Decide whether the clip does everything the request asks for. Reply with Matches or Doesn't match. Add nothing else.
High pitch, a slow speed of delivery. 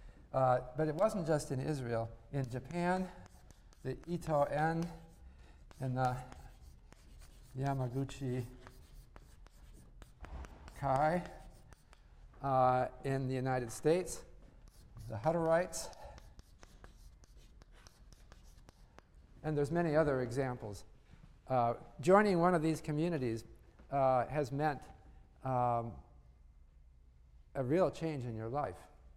Doesn't match